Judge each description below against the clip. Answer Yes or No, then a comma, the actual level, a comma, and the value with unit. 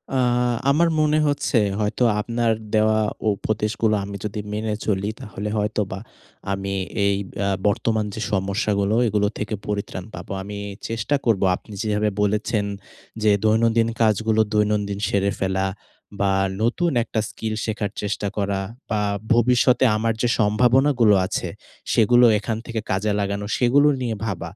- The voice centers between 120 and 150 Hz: No, low, 105 Hz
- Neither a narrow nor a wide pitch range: No, narrow, 2.1 semitones